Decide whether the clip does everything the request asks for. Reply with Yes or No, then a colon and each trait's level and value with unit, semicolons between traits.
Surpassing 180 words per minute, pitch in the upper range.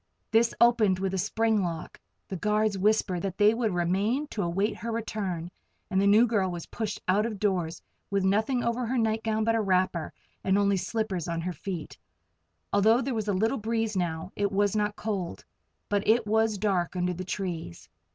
Yes: average, 190 wpm; high, 205 Hz